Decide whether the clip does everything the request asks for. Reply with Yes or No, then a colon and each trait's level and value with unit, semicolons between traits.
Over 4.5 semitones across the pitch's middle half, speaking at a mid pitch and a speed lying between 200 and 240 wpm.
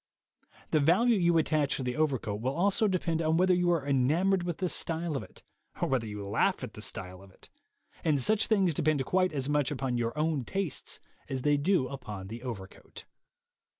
Yes: wide, 5.4 semitones; medium, 150 Hz; fast, 205 wpm